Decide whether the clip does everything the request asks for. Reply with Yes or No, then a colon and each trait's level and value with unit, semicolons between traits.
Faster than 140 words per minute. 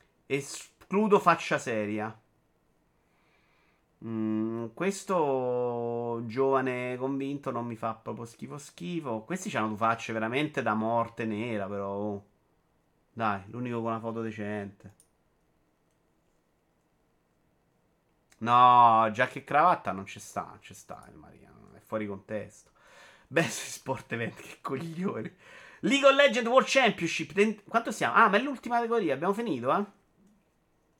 No: average, 125 wpm